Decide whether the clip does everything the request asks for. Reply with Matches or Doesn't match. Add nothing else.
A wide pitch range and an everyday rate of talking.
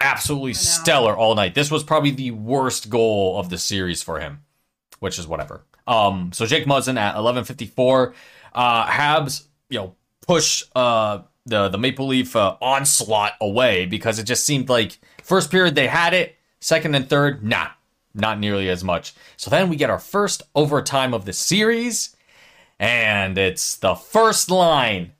Matches